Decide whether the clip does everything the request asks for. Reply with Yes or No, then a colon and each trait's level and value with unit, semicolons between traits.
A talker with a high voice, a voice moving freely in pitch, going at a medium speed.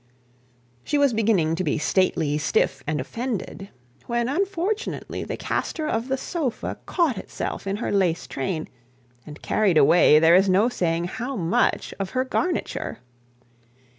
Yes: high, 200 Hz; wide, 7.8 semitones; average, 145 wpm